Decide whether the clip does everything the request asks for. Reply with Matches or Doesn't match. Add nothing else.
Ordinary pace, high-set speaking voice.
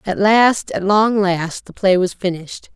Matches